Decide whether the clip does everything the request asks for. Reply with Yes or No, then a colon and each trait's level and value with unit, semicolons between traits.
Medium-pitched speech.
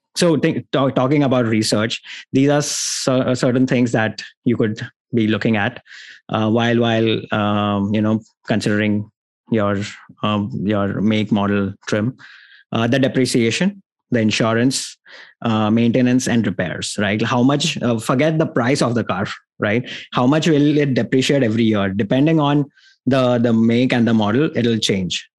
No: low, 120 Hz